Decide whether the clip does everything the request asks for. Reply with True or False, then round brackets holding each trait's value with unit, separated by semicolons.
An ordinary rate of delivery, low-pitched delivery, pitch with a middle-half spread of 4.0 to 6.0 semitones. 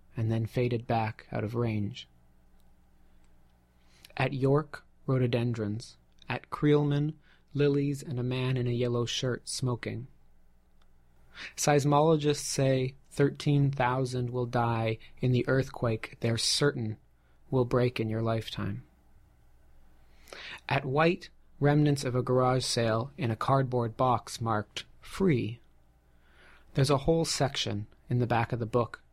False (120 wpm; 120 Hz; 4.9 semitones)